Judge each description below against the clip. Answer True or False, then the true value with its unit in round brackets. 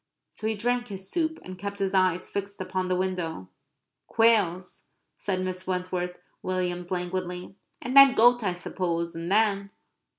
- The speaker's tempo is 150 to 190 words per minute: True (155 wpm)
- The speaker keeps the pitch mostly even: True (2.2 semitones)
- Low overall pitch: False (185 Hz)